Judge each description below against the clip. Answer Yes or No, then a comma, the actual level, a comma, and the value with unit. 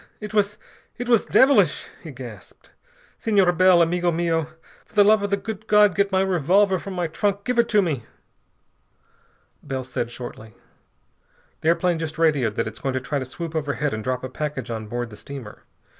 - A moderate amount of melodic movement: No, wide, 7.4 semitones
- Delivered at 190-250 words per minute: Yes, average, 195 wpm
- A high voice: No, medium, 170 Hz